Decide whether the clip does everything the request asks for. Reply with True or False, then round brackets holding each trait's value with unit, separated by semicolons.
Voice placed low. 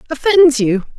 False (275 Hz)